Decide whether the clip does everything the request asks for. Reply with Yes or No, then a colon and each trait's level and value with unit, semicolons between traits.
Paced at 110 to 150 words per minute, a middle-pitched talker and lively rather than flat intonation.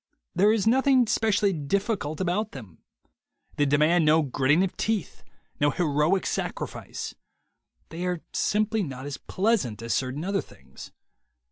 Yes: slow, 135 wpm; medium, 175 Hz; wide, 6.3 semitones